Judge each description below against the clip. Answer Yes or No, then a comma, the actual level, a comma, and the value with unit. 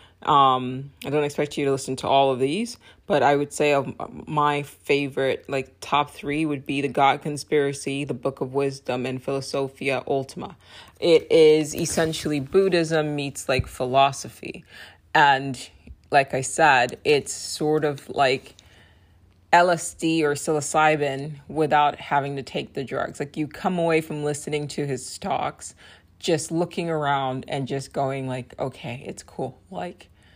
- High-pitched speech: No, medium, 140 Hz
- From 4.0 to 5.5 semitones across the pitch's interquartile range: No, narrow, 2.4 semitones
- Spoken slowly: No, average, 150 wpm